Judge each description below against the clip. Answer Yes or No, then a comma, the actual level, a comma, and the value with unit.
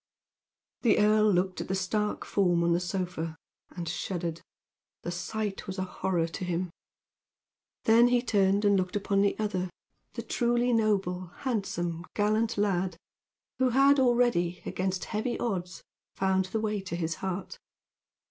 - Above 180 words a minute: No, average, 150 wpm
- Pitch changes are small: No, average, 3.2 semitones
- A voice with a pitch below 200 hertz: Yes, high, 190 Hz